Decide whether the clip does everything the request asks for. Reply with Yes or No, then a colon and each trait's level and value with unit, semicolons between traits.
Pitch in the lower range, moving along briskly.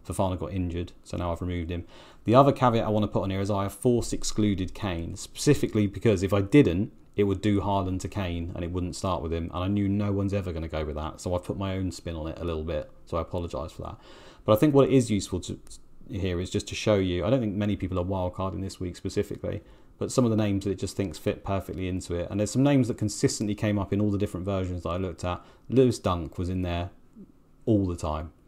Yes: very low, 95 Hz; fast, 275 wpm